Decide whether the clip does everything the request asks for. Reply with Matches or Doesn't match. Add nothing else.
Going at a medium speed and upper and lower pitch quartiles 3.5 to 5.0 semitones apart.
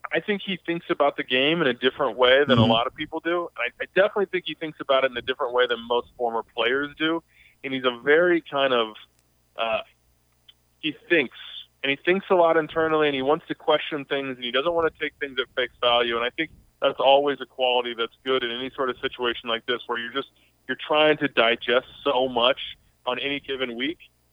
Doesn't match